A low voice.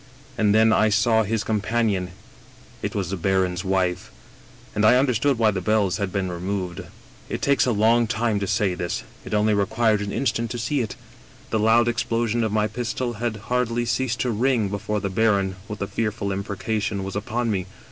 Yes: low, 110 Hz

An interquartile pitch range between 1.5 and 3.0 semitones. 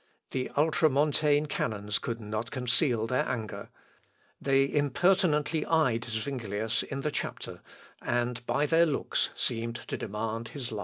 No: average, 4.6 semitones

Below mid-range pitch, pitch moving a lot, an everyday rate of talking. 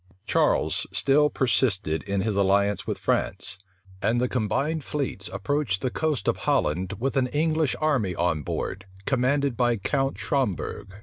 Yes: low, 120 Hz; wide, 6.2 semitones; average, 145 wpm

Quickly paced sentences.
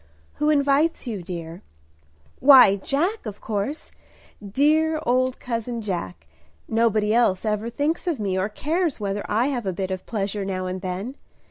No: average, 155 wpm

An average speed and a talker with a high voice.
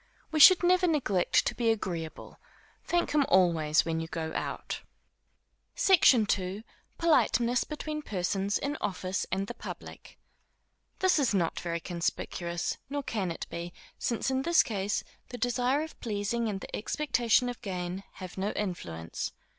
Yes: average, 150 wpm; high, 210 Hz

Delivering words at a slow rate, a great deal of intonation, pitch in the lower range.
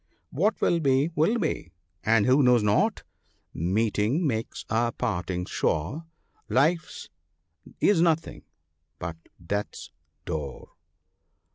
Yes: slow, 120 wpm; wide, 7.7 semitones; low, 120 Hz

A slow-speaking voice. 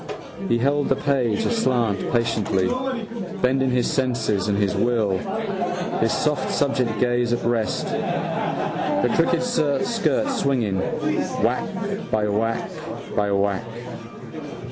Yes: slow, 110 wpm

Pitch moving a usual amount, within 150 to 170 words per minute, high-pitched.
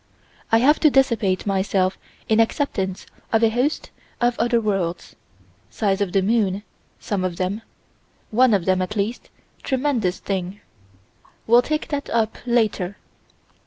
No: average, 4.0 semitones; average, 140 wpm; high, 215 Hz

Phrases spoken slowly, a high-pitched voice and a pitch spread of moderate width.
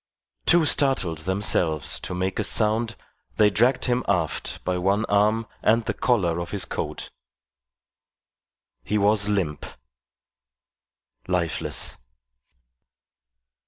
No: slow, 105 wpm; low, 100 Hz; average, 3.6 semitones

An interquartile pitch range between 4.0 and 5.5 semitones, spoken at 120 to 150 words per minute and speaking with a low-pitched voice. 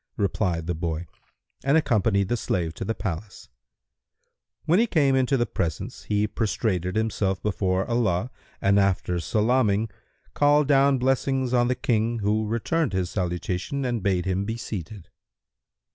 Yes: average, 5.1 semitones; average, 145 wpm; low, 105 Hz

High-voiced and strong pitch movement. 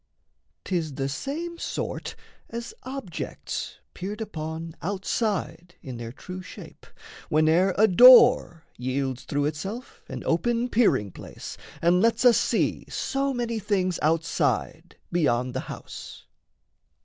No: medium, 180 Hz; wide, 6.7 semitones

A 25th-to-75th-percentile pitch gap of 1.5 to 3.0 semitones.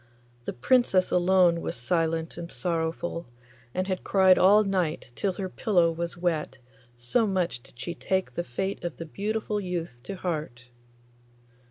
Yes: narrow, 2.6 semitones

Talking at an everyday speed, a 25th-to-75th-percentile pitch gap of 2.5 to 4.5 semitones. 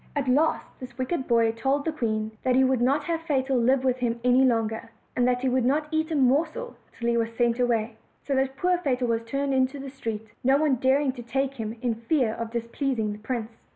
No: fast, 240 wpm; average, 2.9 semitones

